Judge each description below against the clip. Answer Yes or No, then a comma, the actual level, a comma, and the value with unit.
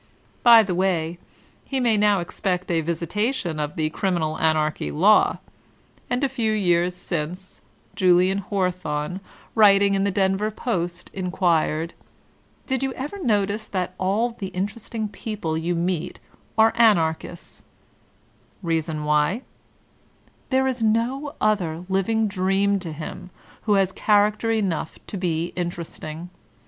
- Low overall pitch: No, high, 190 Hz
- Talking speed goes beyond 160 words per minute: No, slow, 135 wpm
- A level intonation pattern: No, average, 4.0 semitones